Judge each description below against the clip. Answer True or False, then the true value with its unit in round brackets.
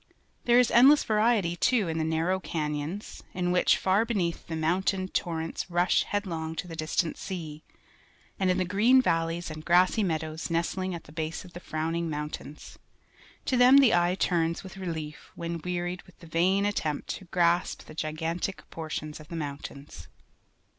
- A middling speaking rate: True (170 wpm)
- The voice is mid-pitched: True (170 Hz)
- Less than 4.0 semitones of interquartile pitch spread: True (2.9 semitones)